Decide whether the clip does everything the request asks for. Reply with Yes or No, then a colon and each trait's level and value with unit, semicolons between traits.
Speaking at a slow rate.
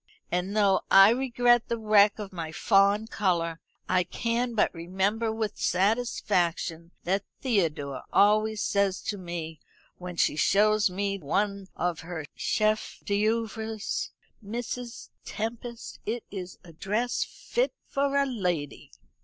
Yes: slow, 130 wpm